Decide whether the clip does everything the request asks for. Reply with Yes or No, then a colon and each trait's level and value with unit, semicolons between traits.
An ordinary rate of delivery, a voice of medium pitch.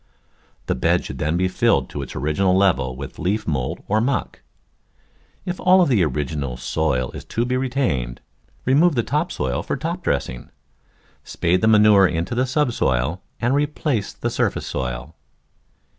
No: average, 160 wpm; very low, 95 Hz